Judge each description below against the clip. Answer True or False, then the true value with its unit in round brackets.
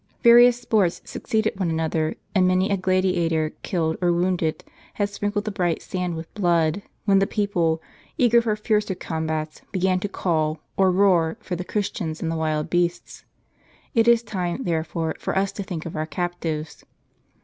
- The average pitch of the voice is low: False (180 Hz)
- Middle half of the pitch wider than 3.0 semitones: True (3.8 semitones)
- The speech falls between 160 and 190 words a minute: True (170 wpm)